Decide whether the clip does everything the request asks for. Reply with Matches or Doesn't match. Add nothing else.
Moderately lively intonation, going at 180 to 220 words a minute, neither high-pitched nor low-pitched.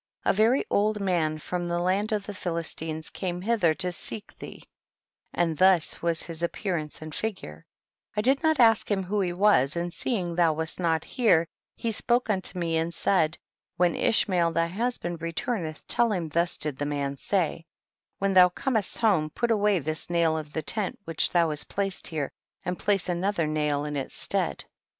Matches